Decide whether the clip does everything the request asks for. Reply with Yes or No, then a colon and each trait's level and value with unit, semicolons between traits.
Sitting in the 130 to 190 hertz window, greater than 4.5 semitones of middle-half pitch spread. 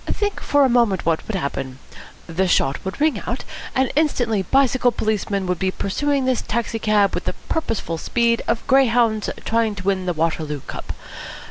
No: high, 220 Hz; average, 5.2 semitones